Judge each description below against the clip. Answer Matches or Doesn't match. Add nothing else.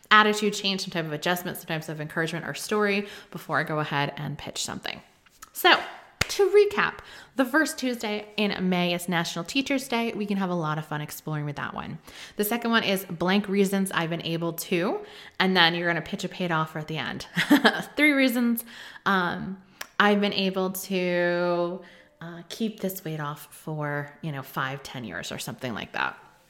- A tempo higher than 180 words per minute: Matches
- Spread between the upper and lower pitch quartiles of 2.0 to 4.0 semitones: Doesn't match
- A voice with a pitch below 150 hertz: Doesn't match